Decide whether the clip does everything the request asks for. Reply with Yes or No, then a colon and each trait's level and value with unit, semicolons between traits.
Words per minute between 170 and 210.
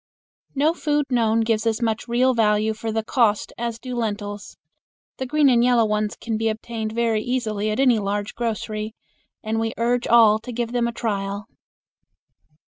Yes: average, 175 wpm